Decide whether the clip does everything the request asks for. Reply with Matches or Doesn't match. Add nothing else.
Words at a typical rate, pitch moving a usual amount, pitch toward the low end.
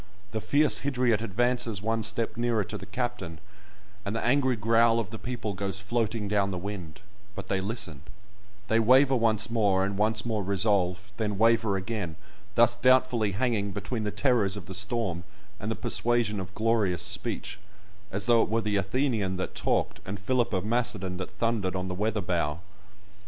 Matches